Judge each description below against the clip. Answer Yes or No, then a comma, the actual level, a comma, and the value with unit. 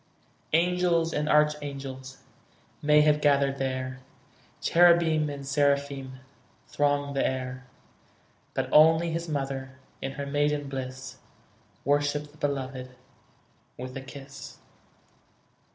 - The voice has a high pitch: No, medium, 140 Hz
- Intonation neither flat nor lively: No, narrow, 2.0 semitones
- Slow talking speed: Yes, slow, 105 wpm